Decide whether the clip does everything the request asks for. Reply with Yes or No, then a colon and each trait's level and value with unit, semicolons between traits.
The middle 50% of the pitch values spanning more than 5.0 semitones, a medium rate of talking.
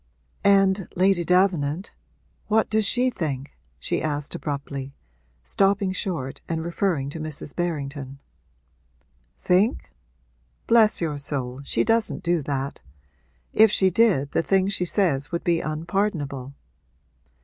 No: wide, 5.5 semitones; slow, 120 wpm